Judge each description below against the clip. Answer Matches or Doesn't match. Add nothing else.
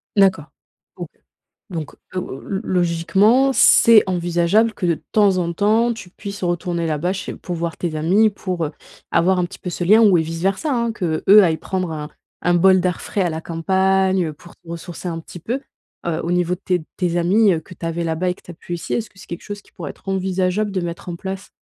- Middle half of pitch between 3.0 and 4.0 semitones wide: Doesn't match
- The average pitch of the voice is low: Doesn't match